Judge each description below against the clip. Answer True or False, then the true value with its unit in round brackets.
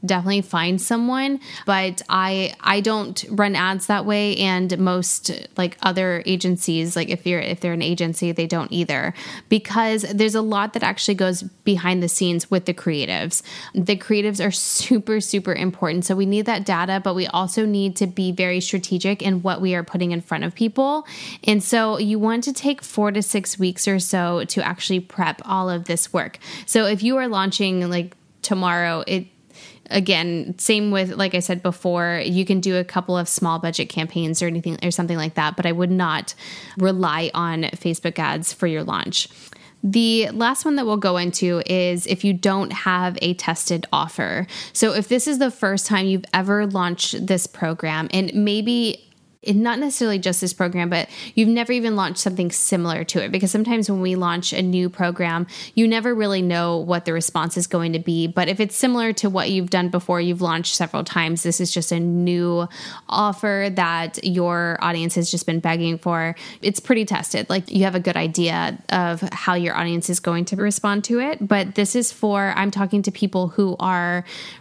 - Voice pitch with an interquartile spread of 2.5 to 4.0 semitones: True (2.9 semitones)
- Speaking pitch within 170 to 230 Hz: True (185 Hz)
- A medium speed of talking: True (195 wpm)